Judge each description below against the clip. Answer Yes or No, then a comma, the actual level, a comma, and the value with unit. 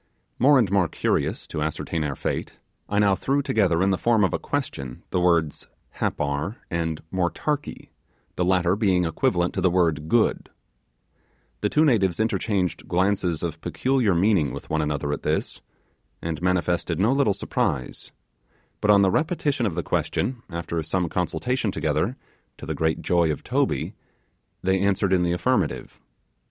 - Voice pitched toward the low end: Yes, very low, 90 Hz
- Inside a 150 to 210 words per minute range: Yes, average, 160 wpm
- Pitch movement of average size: Yes, average, 4.0 semitones